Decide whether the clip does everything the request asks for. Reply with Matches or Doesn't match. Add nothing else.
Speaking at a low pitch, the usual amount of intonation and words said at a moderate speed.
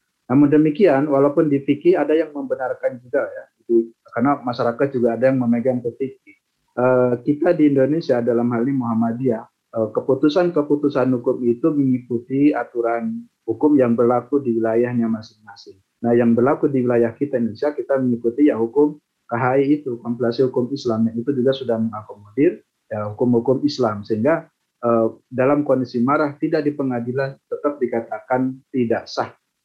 Doesn't match